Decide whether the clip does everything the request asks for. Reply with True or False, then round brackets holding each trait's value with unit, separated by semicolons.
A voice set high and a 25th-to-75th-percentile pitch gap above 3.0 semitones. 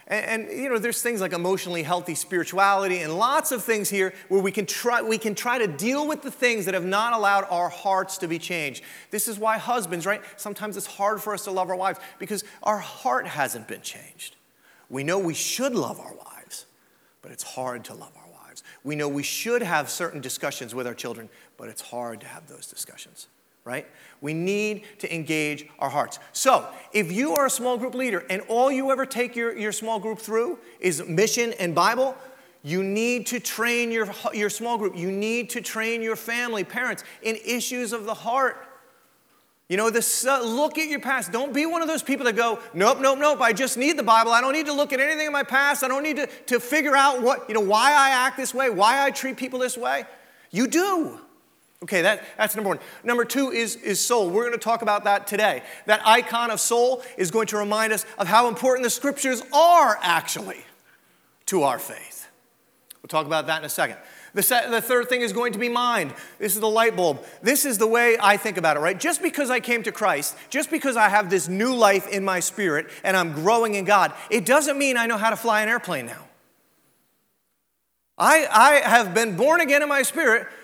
True (225 Hz; 4.4 semitones)